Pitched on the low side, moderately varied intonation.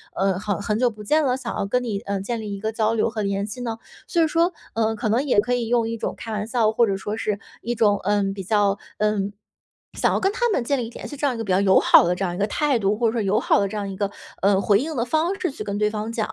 No: high, 215 Hz; average, 3.2 semitones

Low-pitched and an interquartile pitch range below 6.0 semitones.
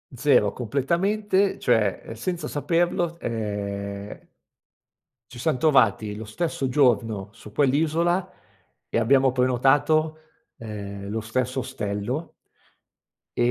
No: low, 130 Hz; wide, 6.6 semitones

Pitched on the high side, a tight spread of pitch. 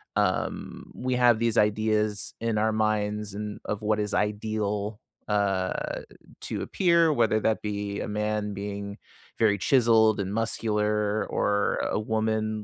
No: low, 105 Hz; narrow, 1.1 semitones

